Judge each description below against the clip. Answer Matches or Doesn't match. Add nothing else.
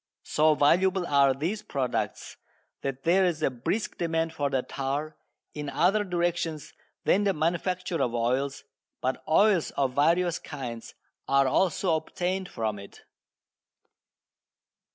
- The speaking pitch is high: Doesn't match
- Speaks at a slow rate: Matches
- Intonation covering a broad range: Doesn't match